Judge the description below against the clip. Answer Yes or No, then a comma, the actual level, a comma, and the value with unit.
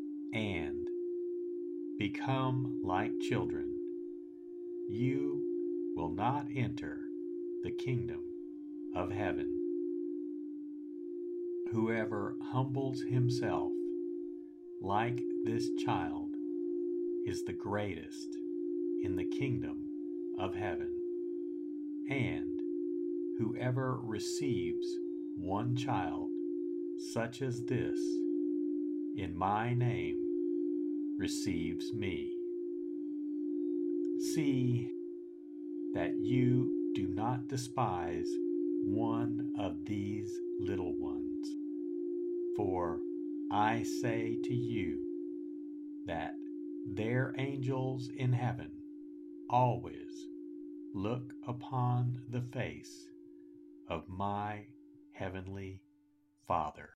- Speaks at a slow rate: Yes, slow, 75 wpm